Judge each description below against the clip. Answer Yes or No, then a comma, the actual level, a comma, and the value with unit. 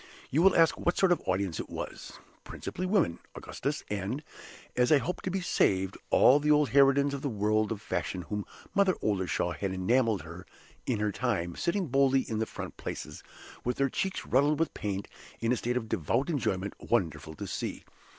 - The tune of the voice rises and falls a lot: Yes, wide, 6.7 semitones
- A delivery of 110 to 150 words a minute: No, average, 190 wpm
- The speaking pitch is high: No, low, 125 Hz